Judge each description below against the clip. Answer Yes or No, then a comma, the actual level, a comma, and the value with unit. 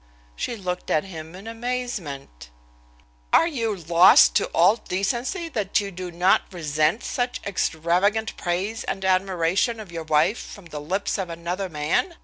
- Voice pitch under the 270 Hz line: Yes, medium, 185 Hz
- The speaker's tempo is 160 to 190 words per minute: No, average, 150 wpm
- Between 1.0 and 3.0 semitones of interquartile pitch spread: No, average, 4.5 semitones